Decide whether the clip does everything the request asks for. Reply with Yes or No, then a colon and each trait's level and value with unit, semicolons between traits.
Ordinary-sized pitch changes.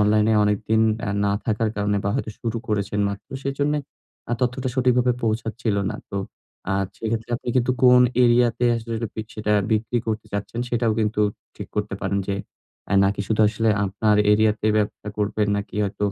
No: narrow, 2.3 semitones